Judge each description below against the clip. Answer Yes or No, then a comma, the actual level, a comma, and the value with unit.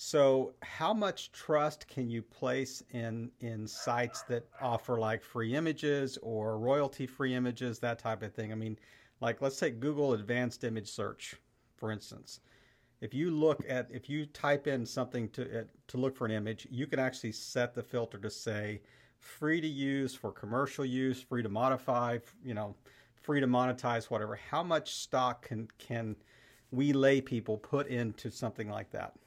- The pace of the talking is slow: No, average, 175 wpm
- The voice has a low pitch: Yes, low, 125 Hz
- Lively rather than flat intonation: No, average, 3.0 semitones